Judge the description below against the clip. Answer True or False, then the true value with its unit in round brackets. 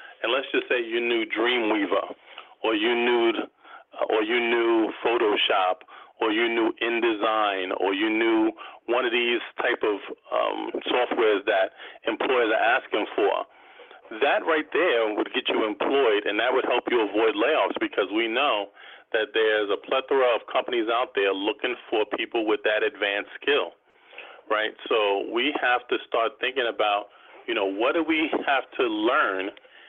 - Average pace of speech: True (165 wpm)